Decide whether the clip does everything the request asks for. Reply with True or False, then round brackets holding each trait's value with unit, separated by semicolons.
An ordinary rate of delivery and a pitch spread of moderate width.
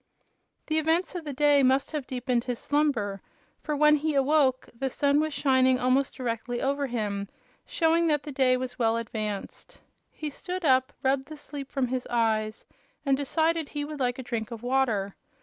True (185 wpm; 3.4 semitones)